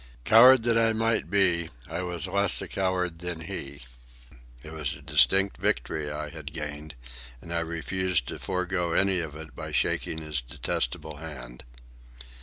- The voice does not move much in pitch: No, average, 3.8 semitones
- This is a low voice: Yes, very low, 85 Hz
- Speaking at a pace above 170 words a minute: No, average, 160 wpm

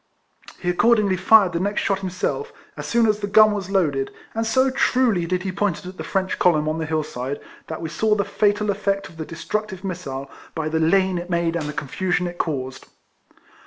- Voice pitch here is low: No, medium, 185 Hz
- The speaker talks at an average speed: No, fast, 215 wpm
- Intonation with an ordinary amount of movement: Yes, average, 4.1 semitones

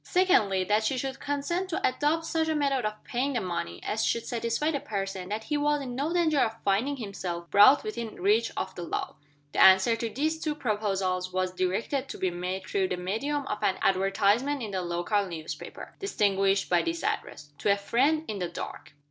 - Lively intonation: Yes, wide, 6.9 semitones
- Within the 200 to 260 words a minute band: Yes, fast, 205 wpm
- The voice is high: Yes, high, 220 Hz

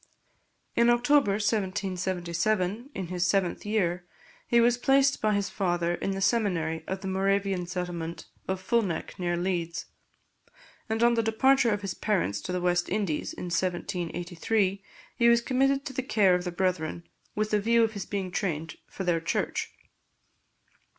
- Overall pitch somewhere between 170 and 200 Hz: Yes, high, 190 Hz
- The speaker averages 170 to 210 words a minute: No, average, 160 wpm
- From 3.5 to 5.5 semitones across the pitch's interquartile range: Yes, average, 3.8 semitones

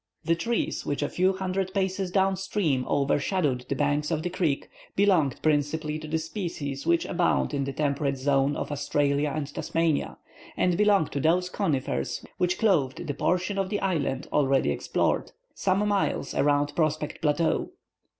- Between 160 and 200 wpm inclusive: Yes, average, 165 wpm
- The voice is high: No, medium, 155 Hz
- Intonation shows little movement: No, average, 4.5 semitones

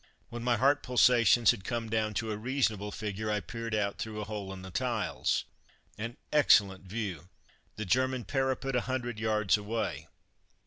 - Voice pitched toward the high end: No, low, 110 Hz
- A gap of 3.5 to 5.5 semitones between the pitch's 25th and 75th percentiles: No, average, 2.9 semitones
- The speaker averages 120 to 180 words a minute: Yes, average, 170 wpm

